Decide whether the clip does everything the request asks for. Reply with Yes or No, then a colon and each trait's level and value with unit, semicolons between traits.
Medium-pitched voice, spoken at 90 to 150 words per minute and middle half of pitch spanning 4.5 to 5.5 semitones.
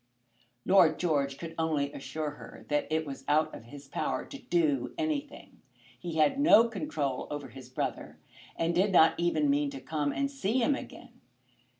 No: medium, 155 Hz; average, 175 wpm; average, 5.2 semitones